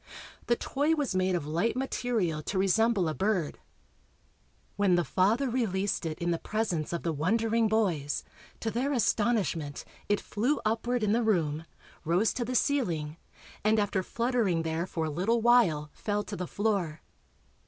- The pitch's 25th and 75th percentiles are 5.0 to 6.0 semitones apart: Yes, wide, 5.5 semitones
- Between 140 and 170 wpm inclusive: Yes, average, 165 wpm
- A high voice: Yes, high, 205 Hz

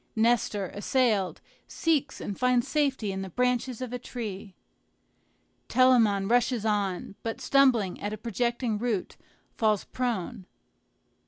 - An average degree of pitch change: Yes, average, 3.6 semitones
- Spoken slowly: Yes, slow, 120 wpm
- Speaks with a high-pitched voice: Yes, high, 230 Hz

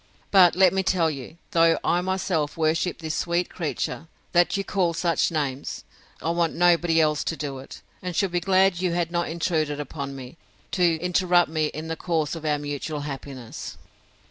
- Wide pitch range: No, average, 2.7 semitones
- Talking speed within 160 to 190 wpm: Yes, average, 185 wpm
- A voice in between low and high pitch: Yes, medium, 165 Hz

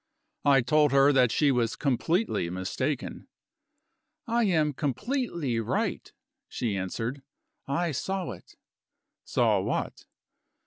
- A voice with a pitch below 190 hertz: Yes, medium, 140 Hz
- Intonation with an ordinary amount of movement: No, wide, 5.7 semitones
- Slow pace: Yes, slow, 105 wpm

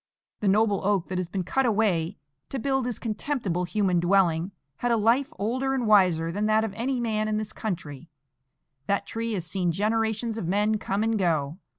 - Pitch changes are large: No, average, 3.7 semitones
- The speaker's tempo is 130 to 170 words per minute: No, average, 195 wpm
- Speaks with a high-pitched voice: Yes, high, 210 Hz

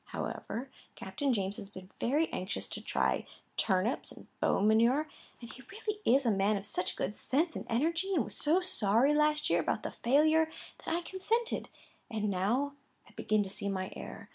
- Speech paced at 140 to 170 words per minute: No, average, 190 wpm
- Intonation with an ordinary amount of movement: No, wide, 7.3 semitones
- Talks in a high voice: Yes, high, 245 Hz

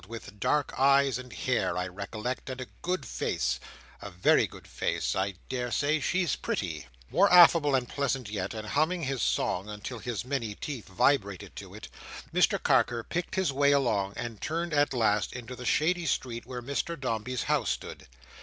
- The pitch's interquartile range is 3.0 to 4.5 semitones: No, average, 5.1 semitones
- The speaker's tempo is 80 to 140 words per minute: No, average, 175 wpm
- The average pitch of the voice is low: Yes, low, 125 Hz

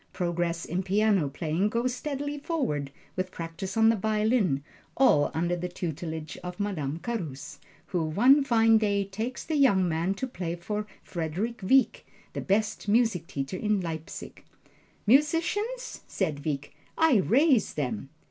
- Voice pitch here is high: Yes, high, 195 Hz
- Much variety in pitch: Yes, wide, 6.0 semitones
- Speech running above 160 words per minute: No, average, 145 wpm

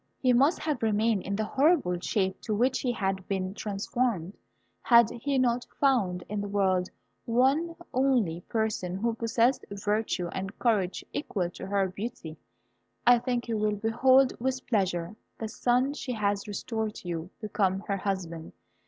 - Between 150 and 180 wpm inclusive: Yes, average, 160 wpm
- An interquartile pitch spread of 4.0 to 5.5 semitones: Yes, average, 4.3 semitones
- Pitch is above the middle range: Yes, high, 215 Hz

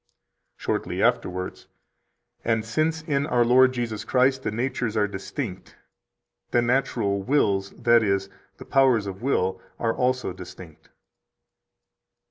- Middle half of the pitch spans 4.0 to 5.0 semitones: Yes, average, 4.6 semitones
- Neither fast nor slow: No, slow, 125 wpm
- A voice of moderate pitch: No, low, 115 Hz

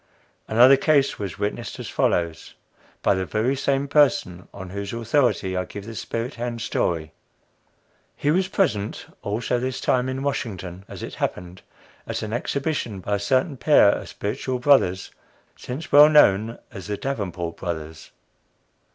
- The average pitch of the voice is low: Yes, low, 115 Hz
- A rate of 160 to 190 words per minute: No, average, 150 wpm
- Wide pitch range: Yes, wide, 6.1 semitones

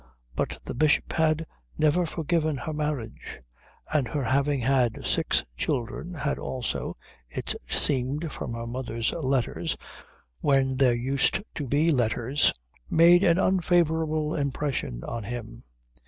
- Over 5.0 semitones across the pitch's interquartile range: No, average, 4.2 semitones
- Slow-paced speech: Yes, slow, 125 wpm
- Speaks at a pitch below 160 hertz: Yes, medium, 140 Hz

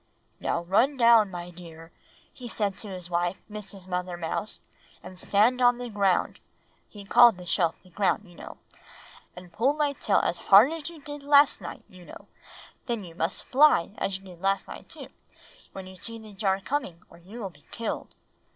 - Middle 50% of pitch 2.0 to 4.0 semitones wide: No, average, 4.8 semitones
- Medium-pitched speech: No, high, 195 Hz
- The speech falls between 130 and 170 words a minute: No, average, 195 wpm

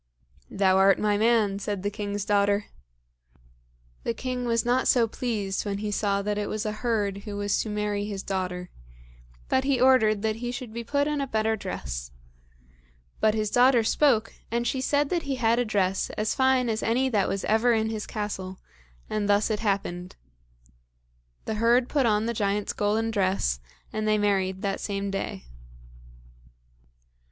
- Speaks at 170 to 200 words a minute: Yes, average, 175 wpm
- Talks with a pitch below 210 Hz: No, high, 215 Hz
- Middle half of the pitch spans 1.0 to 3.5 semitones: Yes, average, 2.7 semitones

